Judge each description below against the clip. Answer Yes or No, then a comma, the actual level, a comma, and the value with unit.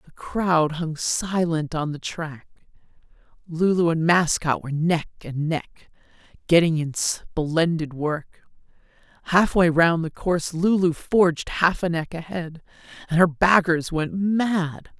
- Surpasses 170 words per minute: No, average, 140 wpm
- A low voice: No, medium, 165 Hz